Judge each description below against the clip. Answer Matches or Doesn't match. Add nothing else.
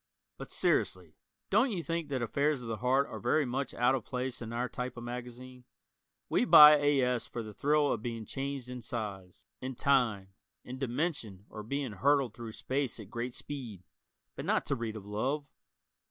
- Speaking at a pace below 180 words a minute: Doesn't match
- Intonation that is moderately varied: Matches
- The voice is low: Matches